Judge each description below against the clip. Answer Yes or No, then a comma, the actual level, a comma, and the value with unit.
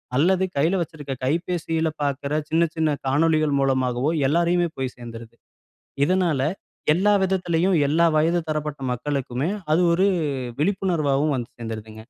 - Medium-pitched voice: Yes, medium, 155 Hz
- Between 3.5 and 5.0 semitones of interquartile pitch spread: Yes, average, 4.0 semitones